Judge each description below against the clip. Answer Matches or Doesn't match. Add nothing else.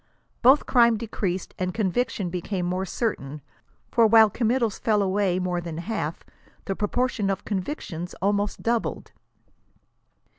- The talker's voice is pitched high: Matches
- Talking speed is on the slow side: Matches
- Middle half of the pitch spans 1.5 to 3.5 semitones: Doesn't match